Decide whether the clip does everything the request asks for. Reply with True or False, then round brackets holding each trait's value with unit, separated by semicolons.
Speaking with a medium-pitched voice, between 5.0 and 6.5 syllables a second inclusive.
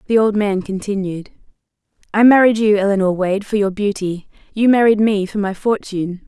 False (205 Hz; 5.4 syllables/s)